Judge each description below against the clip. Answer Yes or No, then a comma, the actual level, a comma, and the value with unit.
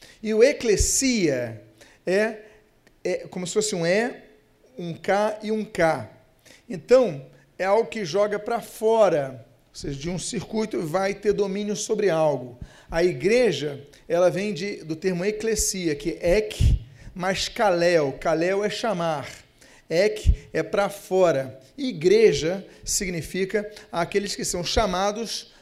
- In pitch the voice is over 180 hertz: Yes, high, 190 Hz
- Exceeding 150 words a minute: No, average, 135 wpm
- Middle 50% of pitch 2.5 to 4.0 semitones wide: No, average, 4.8 semitones